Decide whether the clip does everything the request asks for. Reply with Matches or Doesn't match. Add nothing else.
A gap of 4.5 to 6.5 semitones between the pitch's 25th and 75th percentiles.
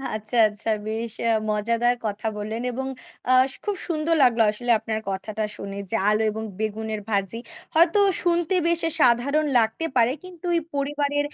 Matches